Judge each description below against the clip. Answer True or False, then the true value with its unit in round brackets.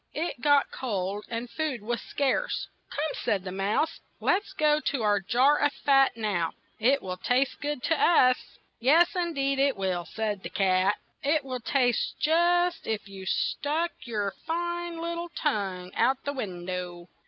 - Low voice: False (255 Hz)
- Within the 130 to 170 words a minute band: False (180 wpm)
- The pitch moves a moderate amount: False (7.2 semitones)